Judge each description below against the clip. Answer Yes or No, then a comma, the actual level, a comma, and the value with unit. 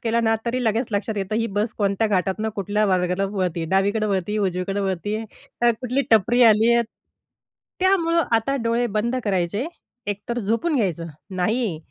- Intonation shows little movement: No, average, 3.5 semitones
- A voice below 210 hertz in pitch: No, high, 215 Hz